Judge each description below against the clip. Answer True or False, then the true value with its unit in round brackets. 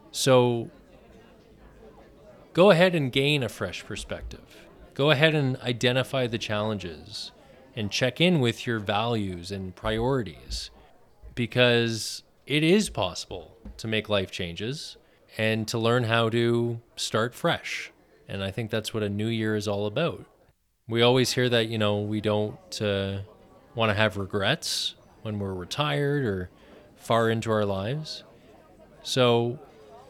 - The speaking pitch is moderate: False (115 Hz)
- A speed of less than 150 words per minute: True (140 wpm)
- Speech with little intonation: False (3.4 semitones)